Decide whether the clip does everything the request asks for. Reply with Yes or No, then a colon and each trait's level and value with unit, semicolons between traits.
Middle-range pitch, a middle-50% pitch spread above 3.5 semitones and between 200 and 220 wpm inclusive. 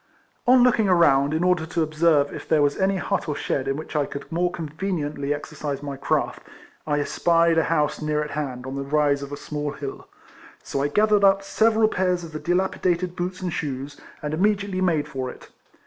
Yes: medium, 155 Hz; average, 4.0 semitones; fast, 205 wpm